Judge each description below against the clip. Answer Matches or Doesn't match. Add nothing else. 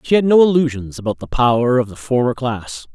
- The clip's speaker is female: Doesn't match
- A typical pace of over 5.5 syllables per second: Matches